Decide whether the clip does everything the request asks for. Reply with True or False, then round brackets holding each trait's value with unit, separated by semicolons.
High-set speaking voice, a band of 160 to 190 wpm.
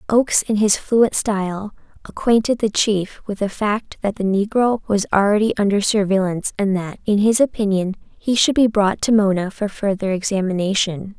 True (205 Hz; 170 wpm)